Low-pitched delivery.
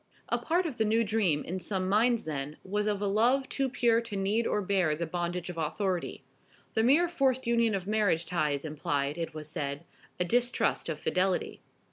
No: high, 195 Hz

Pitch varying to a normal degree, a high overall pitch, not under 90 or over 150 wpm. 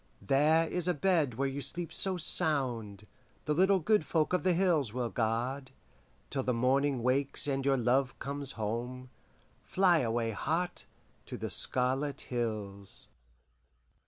No: average, 4.7 semitones; low, 135 Hz; average, 145 wpm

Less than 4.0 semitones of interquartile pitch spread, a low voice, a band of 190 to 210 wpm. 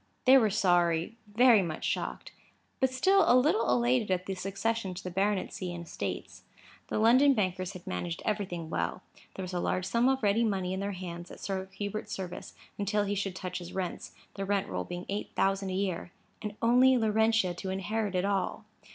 No: average, 3.4 semitones; high, 195 Hz; average, 195 wpm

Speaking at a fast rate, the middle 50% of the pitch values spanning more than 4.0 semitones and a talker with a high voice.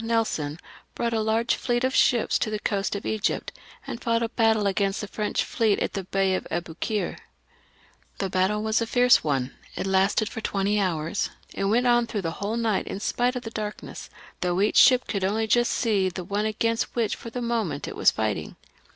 No: fast, 210 wpm; average, 3.0 semitones; high, 210 Hz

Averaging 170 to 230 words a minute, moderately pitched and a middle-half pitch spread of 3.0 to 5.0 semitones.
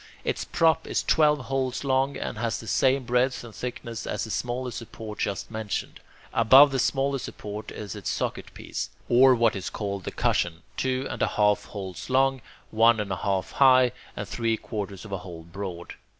No: average, 190 wpm; low, 115 Hz; average, 4.3 semitones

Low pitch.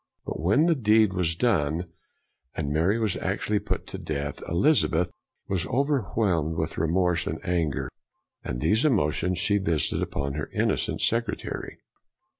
Yes: very low, 90 Hz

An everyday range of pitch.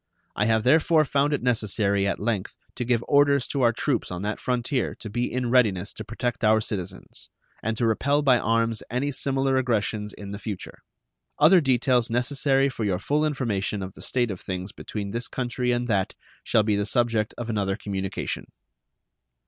Yes: average, 3.8 semitones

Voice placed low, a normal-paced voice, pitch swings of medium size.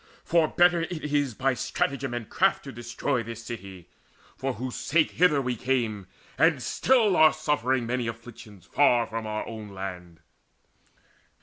Yes: low, 120 Hz; average, 160 wpm; average, 4.7 semitones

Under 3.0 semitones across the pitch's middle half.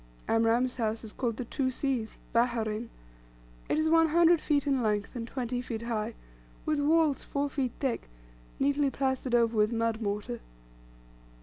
No: average, 3.7 semitones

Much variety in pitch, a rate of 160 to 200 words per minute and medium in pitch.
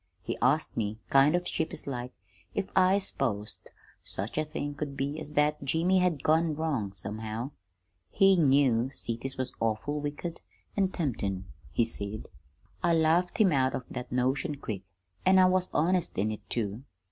Yes: wide, 5.8 semitones; average, 165 wpm; medium, 145 Hz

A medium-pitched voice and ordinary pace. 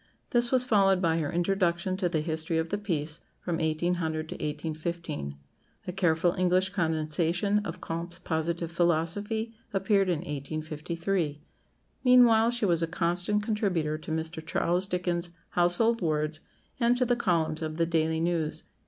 Yes: medium, 170 Hz; average, 150 wpm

